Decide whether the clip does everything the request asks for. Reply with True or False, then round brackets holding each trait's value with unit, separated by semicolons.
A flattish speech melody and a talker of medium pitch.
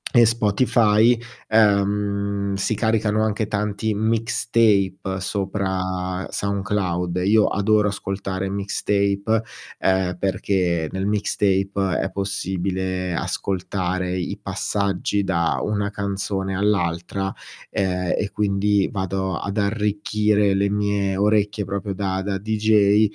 False (1.6 semitones; 100 Hz)